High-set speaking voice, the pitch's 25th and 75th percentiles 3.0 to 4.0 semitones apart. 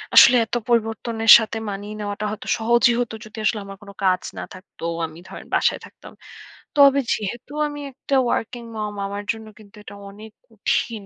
No: high, 220 Hz; narrow, 2.6 semitones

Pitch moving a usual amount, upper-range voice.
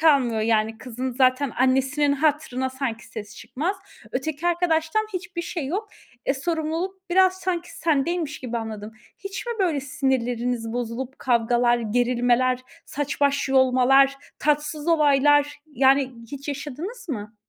Yes: average, 4.3 semitones; very high, 275 Hz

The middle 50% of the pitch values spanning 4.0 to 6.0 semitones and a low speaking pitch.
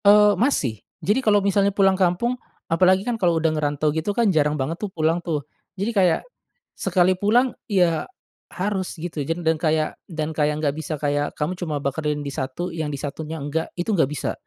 No: average, 4.3 semitones; medium, 165 Hz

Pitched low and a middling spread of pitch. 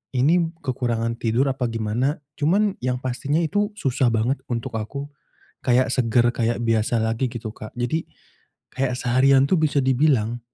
Yes: low, 125 Hz; average, 3.2 semitones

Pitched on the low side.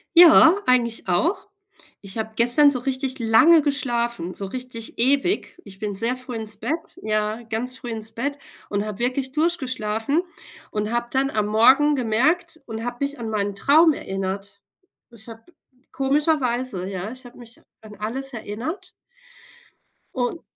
No: high, 240 Hz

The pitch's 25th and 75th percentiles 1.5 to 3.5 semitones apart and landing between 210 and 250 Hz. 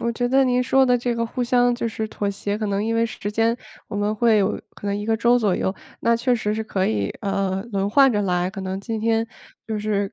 Yes: average, 2.8 semitones; high, 220 Hz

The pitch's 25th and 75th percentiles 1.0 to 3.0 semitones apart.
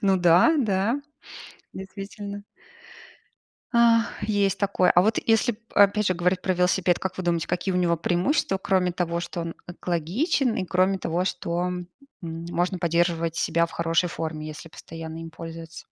Yes: narrow, 2.6 semitones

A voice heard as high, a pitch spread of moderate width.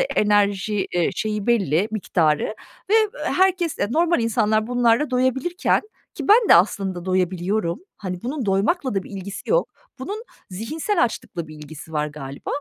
No: high, 210 Hz; wide, 6.5 semitones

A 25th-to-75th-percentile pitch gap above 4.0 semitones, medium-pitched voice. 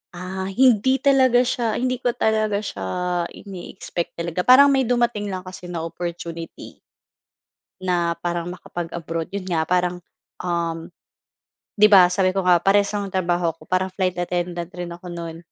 No: average, 3.2 semitones; medium, 180 Hz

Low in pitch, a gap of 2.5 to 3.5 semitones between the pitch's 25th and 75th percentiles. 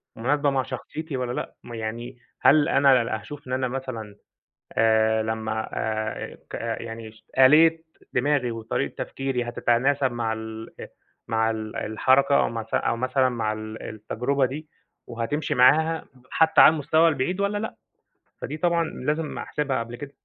No: low, 125 Hz; average, 4.5 semitones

